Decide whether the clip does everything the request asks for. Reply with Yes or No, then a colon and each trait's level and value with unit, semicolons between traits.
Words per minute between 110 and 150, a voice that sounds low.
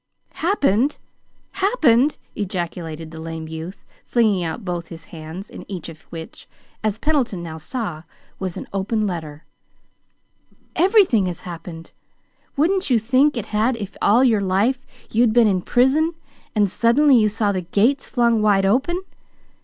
No: average, 145 wpm; high, 210 Hz